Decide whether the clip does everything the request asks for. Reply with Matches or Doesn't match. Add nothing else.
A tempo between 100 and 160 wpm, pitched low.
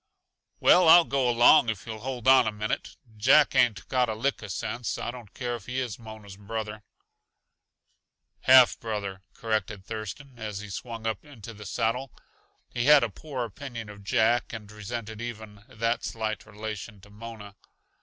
Doesn't match